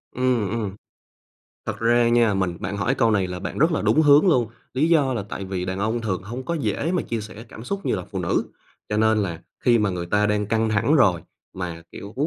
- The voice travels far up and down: No, average, 4.6 semitones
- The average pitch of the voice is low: Yes, low, 110 Hz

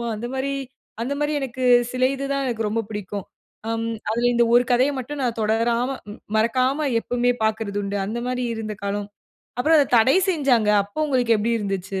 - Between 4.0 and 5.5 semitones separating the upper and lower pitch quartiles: No, average, 3.2 semitones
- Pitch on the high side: Yes, high, 235 Hz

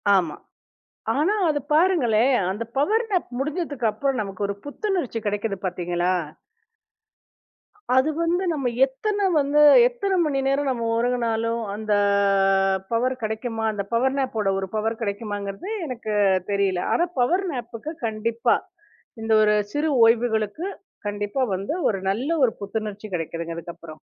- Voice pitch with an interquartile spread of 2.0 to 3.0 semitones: No, wide, 5.6 semitones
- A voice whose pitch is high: Yes, high, 230 Hz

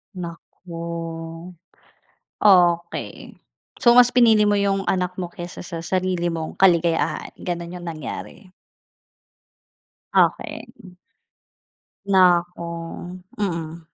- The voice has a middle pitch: Yes, medium, 175 Hz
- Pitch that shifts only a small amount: Yes, narrow, 2.0 semitones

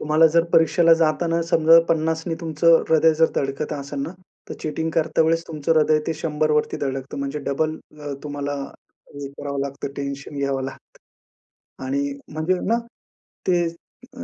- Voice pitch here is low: No, medium, 155 Hz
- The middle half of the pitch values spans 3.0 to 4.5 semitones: No, narrow, 2.4 semitones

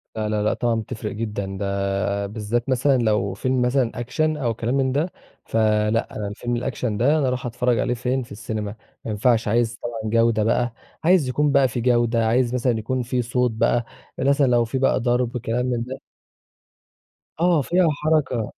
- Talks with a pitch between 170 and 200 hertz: No, low, 120 Hz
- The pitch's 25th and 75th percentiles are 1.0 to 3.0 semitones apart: Yes, average, 2.7 semitones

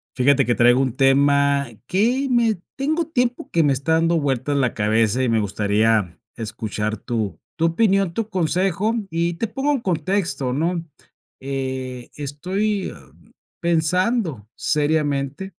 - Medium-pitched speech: Yes, medium, 145 Hz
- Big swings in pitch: Yes, wide, 6.8 semitones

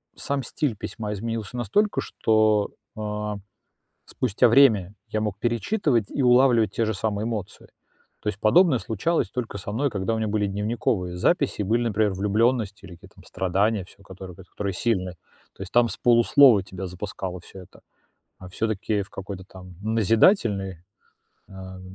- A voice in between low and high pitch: No, low, 105 Hz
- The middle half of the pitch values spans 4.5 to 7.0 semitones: No, average, 3.3 semitones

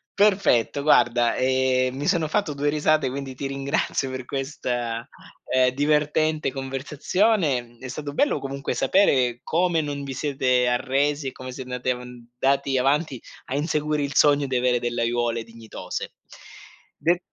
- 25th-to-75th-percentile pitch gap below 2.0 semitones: No, average, 2.8 semitones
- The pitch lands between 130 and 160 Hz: Yes, low, 135 Hz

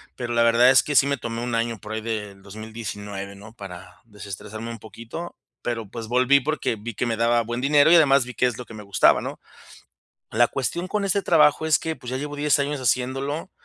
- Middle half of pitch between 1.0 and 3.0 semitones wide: No, average, 4.2 semitones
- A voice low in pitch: Yes, low, 120 Hz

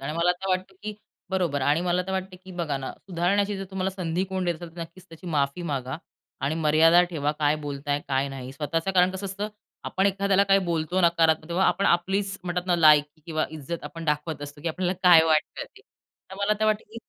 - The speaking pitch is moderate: Yes, medium, 170 Hz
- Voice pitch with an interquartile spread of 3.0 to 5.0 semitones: Yes, average, 3.6 semitones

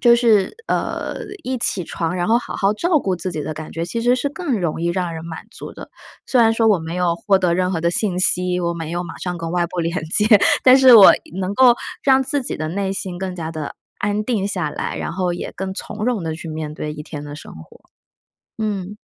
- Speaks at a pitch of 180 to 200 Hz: Yes, medium, 185 Hz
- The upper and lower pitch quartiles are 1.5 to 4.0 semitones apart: No, average, 4.5 semitones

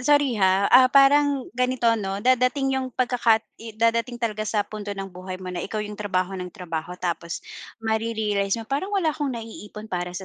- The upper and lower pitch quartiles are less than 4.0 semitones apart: No, average, 4.7 semitones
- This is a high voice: Yes, high, 220 Hz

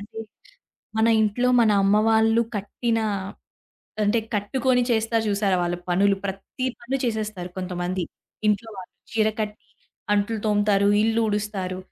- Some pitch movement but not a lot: No, narrow, 2.3 semitones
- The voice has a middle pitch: No, high, 210 Hz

